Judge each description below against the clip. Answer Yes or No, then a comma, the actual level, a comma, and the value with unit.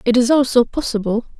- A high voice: Yes, high, 240 Hz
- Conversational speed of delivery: Yes, average, 170 wpm